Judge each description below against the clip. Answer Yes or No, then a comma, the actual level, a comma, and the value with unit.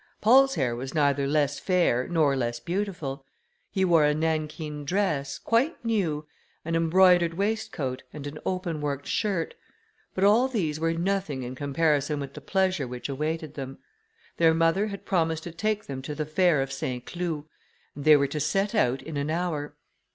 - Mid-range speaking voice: Yes, medium, 160 Hz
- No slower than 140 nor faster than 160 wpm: No, average, 175 wpm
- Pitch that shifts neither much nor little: Yes, average, 4.6 semitones